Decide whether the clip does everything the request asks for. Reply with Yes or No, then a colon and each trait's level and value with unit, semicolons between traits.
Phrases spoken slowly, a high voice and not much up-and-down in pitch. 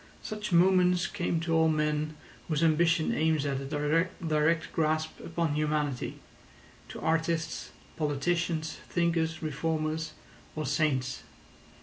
No: slow, 105 wpm; medium, 160 Hz; narrow, 1.6 semitones